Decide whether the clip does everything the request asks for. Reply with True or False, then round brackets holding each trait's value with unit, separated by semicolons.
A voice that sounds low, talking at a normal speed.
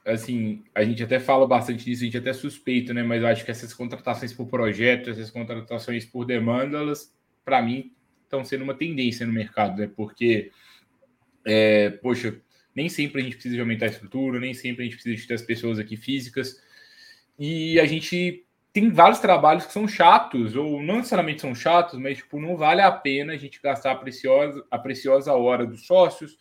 False (125 Hz; 200 wpm)